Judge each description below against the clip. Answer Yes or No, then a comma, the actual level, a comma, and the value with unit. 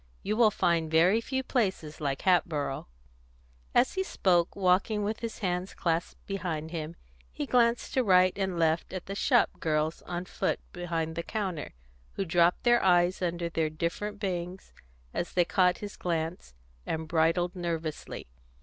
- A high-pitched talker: No, medium, 175 Hz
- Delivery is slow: No, average, 160 wpm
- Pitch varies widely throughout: No, average, 3.3 semitones